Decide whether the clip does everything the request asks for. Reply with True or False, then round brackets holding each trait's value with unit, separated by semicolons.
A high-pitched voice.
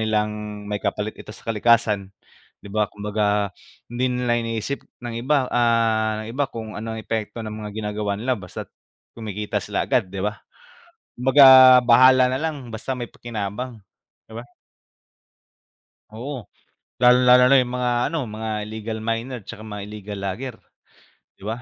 False (110 Hz)